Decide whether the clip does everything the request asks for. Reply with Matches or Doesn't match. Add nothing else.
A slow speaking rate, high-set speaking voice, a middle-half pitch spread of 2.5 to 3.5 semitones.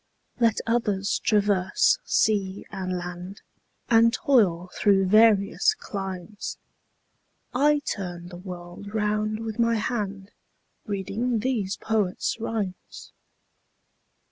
Matches